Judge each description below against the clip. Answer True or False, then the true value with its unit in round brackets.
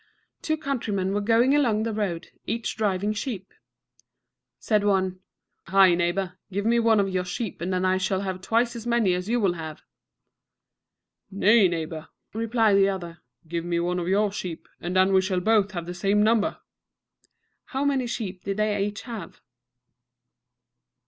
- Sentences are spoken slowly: False (165 wpm)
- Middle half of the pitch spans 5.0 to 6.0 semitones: False (3.4 semitones)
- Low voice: False (195 Hz)